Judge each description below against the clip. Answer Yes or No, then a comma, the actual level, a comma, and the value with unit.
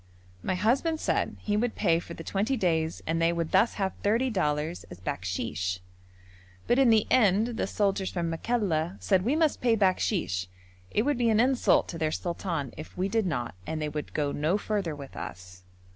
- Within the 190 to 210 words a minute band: Yes, average, 195 wpm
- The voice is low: No, medium, 185 Hz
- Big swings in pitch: Yes, wide, 5.8 semitones